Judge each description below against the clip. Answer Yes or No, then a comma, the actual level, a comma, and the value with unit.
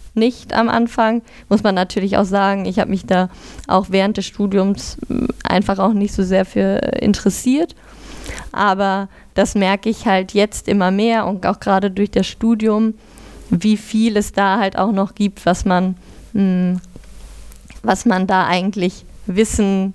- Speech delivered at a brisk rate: No, average, 155 wpm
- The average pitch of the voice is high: Yes, high, 195 Hz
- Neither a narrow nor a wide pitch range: No, narrow, 2.1 semitones